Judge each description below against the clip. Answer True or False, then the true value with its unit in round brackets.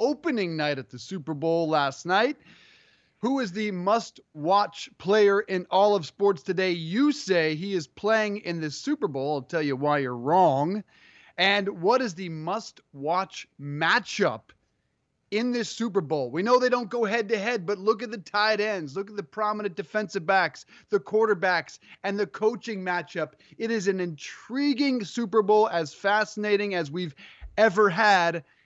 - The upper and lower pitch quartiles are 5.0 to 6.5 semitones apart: False (4.6 semitones)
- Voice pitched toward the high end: True (200 Hz)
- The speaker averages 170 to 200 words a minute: True (175 wpm)